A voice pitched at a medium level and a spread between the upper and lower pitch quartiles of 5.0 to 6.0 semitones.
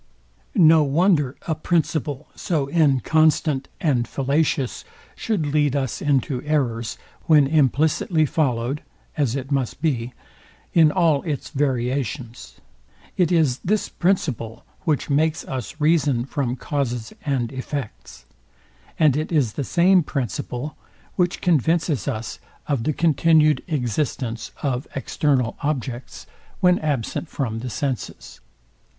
No: medium, 145 Hz; average, 3.7 semitones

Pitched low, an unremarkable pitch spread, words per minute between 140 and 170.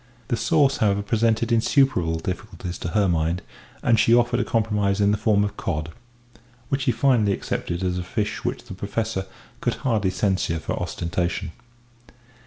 Yes: low, 105 Hz; average, 4.1 semitones; average, 165 wpm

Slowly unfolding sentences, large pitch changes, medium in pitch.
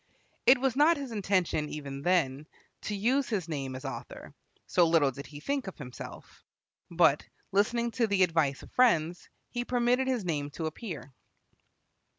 No: average, 165 wpm; wide, 8.3 semitones; medium, 180 Hz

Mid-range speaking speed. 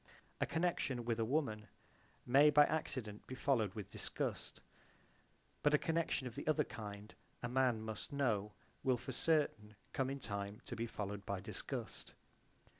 Yes: average, 160 wpm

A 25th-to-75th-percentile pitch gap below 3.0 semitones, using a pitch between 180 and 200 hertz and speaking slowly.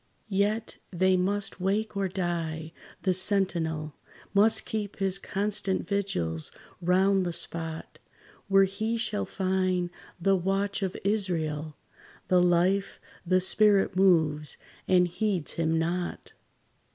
Yes: narrow, 2.6 semitones; medium, 185 Hz; slow, 115 wpm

